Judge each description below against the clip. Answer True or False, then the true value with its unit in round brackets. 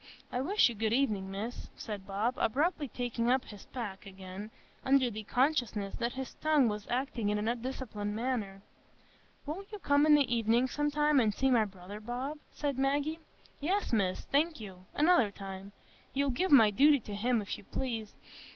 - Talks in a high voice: True (240 Hz)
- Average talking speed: True (180 wpm)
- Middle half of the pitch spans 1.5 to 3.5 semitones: False (5.2 semitones)